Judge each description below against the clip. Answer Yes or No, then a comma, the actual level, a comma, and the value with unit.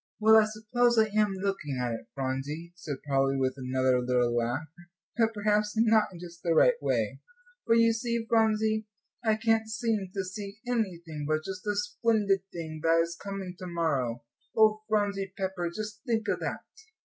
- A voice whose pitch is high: Yes, high, 195 Hz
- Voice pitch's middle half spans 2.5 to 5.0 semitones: No, wide, 5.6 semitones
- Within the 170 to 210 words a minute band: Yes, average, 175 wpm